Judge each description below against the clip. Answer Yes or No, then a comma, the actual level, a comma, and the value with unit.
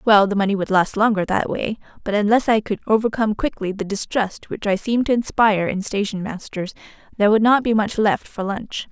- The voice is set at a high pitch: Yes, high, 210 Hz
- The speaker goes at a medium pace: No, fast, 215 wpm